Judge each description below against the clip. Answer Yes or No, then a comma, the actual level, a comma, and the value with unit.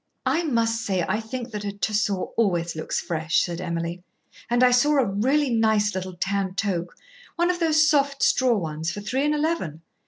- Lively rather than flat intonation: Yes, wide, 6.2 semitones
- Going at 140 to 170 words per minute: No, average, 190 wpm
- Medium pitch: No, high, 210 Hz